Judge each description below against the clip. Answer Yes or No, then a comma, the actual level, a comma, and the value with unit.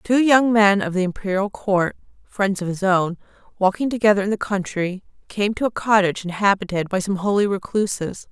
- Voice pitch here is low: No, high, 200 Hz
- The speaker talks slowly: No, average, 180 wpm